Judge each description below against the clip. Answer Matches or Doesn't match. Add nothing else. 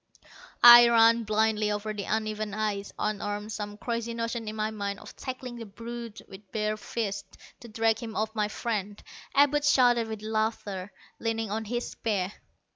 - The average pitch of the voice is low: Doesn't match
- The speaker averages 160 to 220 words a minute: Matches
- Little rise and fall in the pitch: Matches